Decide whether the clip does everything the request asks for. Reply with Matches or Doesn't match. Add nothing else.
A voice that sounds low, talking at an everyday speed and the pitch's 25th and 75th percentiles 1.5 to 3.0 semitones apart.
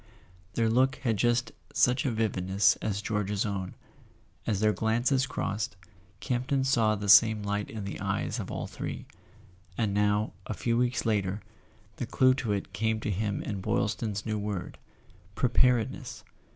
Matches